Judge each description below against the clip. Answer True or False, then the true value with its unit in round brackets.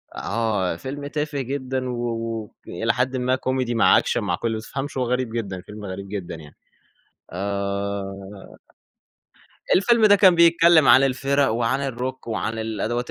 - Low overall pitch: True (120 Hz)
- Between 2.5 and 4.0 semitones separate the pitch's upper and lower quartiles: False (4.5 semitones)